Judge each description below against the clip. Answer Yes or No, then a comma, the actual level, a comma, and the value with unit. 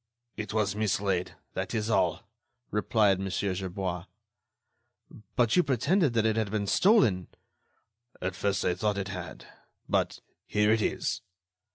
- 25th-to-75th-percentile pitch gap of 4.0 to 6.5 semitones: No, average, 2.8 semitones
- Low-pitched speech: Yes, low, 105 Hz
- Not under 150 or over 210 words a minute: No, average, 140 wpm